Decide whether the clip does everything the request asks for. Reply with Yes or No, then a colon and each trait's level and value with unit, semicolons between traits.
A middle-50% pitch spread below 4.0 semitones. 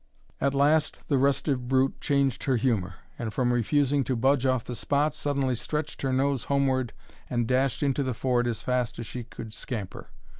Yes: narrow, 2.4 semitones